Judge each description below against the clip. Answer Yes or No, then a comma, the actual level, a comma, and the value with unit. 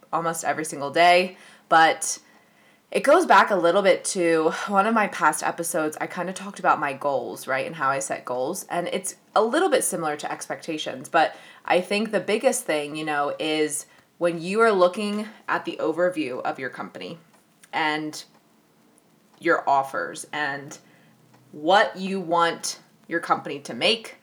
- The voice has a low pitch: No, medium, 170 Hz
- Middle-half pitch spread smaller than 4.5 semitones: Yes, average, 3.7 semitones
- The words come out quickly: No, average, 170 wpm